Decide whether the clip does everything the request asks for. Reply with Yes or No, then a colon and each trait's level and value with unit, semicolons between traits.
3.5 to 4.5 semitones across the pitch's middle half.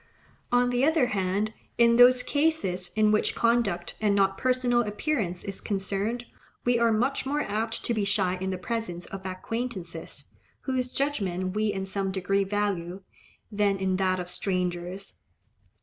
Yes: average, 4.2 semitones